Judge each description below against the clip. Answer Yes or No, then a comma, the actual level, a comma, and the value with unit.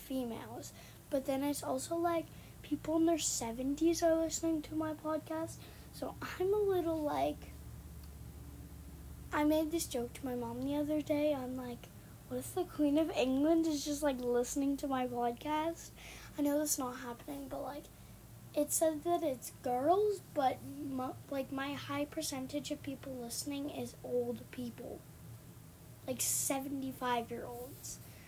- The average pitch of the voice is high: Yes, very high, 280 Hz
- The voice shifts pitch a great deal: No, average, 3.8 semitones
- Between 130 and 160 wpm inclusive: Yes, average, 155 wpm